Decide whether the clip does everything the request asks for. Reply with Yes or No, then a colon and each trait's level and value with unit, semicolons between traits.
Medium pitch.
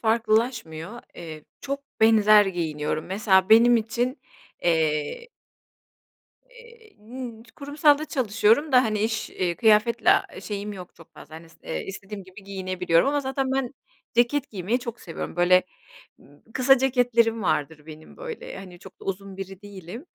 No: high, 215 Hz